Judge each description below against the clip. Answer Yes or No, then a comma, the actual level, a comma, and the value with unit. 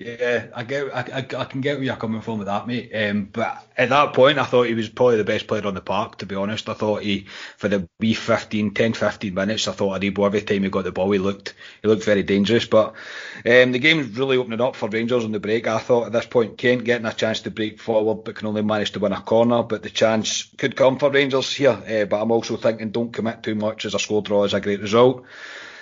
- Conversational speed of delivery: No, fast, 270 wpm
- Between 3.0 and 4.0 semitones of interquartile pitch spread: No, narrow, 2.5 semitones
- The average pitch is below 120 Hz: Yes, low, 110 Hz